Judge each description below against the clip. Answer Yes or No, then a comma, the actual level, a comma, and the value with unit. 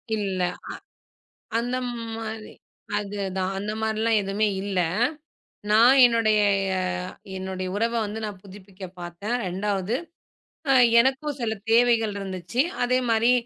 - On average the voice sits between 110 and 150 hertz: No, high, 215 Hz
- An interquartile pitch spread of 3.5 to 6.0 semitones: No, average, 3.0 semitones